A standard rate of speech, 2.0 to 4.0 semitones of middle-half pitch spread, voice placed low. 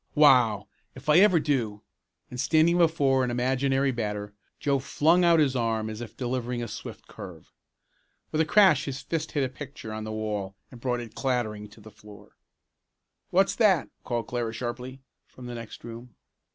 No: average, 180 wpm; average, 4.5 semitones; low, 125 Hz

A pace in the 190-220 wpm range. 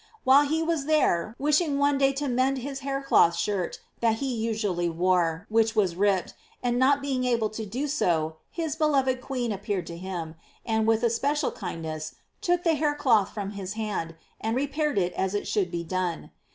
Yes: average, 200 wpm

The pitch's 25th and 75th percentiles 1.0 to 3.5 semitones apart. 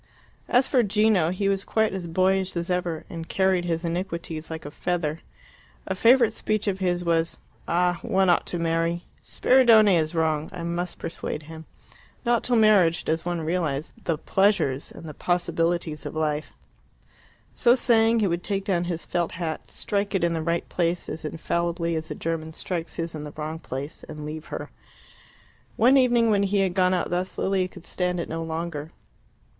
Yes: average, 2.9 semitones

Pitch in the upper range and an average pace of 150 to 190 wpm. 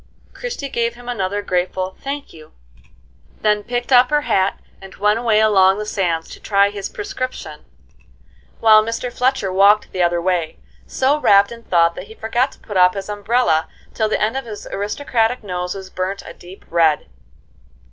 Yes: high, 205 Hz; average, 175 wpm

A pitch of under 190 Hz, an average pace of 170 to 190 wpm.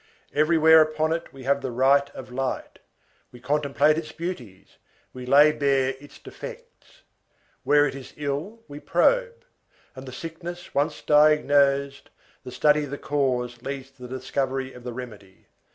No: medium, 140 Hz; average, 155 wpm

